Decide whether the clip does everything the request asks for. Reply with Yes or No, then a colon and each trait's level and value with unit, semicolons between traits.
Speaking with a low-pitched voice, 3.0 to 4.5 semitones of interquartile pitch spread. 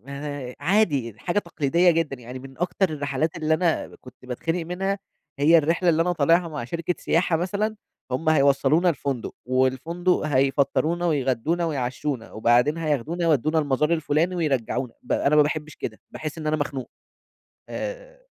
No: medium, 155 Hz; average, 4.1 semitones